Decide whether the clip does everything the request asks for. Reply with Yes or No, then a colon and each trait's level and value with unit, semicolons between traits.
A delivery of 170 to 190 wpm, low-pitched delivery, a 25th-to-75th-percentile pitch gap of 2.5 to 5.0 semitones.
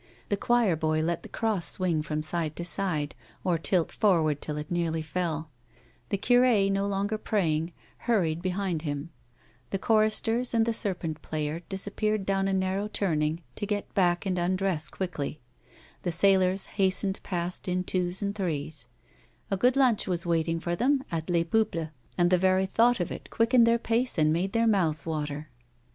No: average, 175 wpm; medium, 185 Hz; average, 3.9 semitones